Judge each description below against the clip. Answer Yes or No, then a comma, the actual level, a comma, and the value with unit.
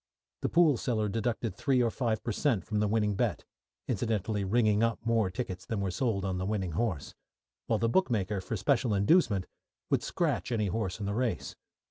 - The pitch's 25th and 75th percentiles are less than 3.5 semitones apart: Yes, average, 3.0 semitones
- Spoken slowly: No, average, 190 wpm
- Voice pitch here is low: Yes, low, 110 Hz